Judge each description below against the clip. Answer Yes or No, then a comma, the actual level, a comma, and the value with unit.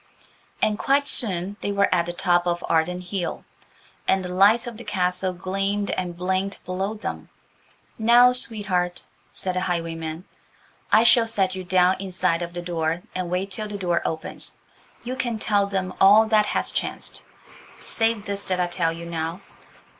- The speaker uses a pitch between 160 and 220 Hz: Yes, medium, 185 Hz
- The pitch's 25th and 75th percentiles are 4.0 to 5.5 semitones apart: No, average, 2.8 semitones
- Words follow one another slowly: No, average, 175 wpm